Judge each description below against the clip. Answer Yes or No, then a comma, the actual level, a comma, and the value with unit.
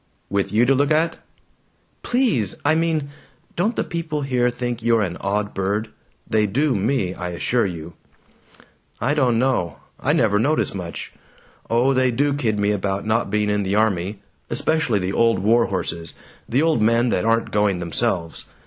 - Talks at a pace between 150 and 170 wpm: Yes, average, 165 wpm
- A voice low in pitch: Yes, low, 115 Hz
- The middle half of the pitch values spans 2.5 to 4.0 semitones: No, average, 5.1 semitones